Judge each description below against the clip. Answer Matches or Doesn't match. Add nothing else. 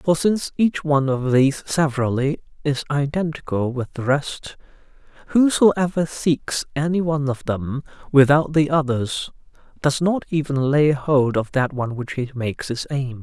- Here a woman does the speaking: Doesn't match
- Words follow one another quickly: Doesn't match